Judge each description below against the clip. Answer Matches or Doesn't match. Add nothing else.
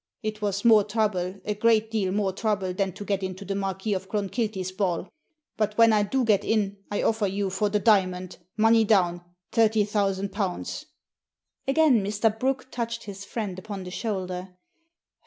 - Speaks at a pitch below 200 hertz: Doesn't match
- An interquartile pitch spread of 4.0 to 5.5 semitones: Doesn't match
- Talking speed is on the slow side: Doesn't match